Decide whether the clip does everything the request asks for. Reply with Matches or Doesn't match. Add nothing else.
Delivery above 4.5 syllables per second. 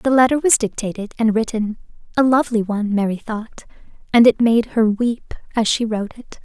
Matches